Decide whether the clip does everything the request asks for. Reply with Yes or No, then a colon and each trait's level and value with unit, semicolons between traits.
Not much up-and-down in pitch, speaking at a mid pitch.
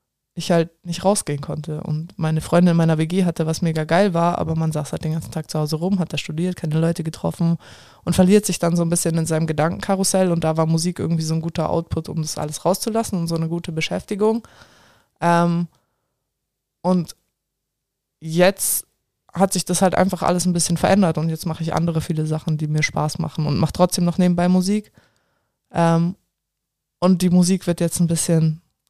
Yes: narrow, 2.1 semitones; medium, 170 Hz